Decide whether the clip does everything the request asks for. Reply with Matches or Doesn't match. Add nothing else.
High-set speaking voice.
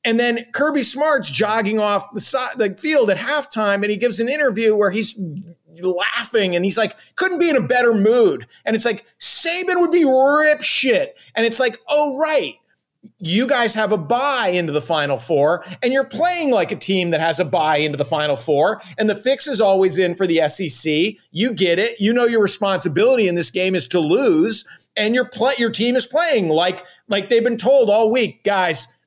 Matches